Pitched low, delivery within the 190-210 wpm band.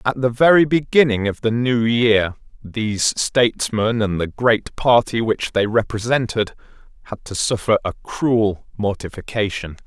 No: low, 115 Hz; average, 140 wpm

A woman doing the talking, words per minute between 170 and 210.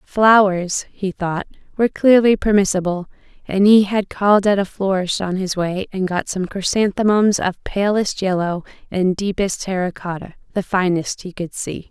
No: female; average, 160 wpm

